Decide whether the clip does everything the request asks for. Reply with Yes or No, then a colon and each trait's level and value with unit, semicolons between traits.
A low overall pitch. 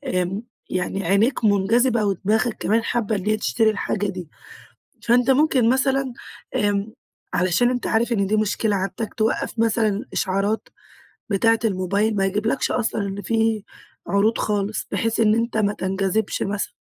No: high, 215 Hz